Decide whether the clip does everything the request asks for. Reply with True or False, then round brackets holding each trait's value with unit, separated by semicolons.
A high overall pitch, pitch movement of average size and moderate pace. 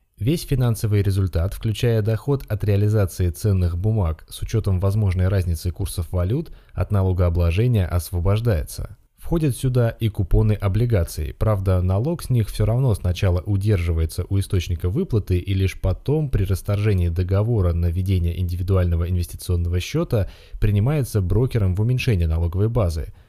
False (100 Hz; 3.5 semitones; 130 wpm)